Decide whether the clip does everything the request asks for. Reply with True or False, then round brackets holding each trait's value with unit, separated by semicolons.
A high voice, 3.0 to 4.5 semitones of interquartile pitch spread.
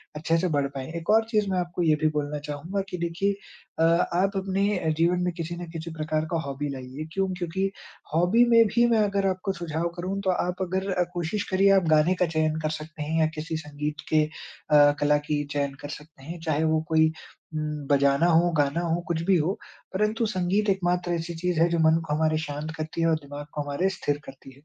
False (165 Hz; 3.5 semitones)